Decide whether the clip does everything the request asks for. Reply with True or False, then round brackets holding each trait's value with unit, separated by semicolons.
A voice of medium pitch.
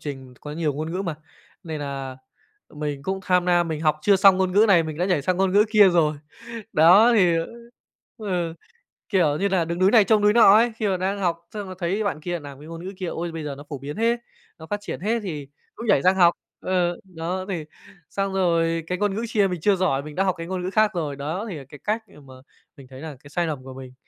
True (175 Hz)